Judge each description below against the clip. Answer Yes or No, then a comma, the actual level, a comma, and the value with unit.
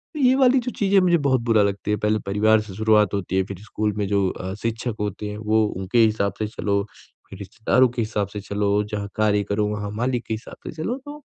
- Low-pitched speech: Yes, low, 105 Hz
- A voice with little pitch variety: Yes, narrow, 2.3 semitones